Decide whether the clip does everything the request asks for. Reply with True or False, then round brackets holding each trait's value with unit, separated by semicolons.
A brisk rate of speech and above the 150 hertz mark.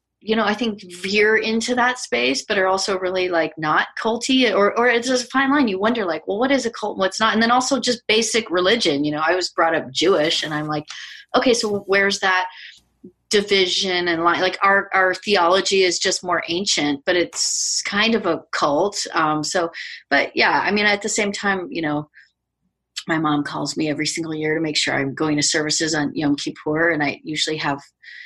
True (220 wpm; 190 Hz)